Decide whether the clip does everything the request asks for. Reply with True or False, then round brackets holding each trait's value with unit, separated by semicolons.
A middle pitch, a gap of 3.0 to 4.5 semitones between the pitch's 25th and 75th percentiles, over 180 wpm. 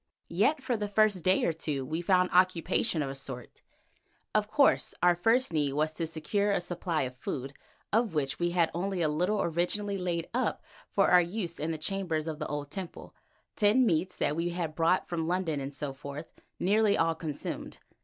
True (170 Hz; 3.8 semitones; 200 wpm)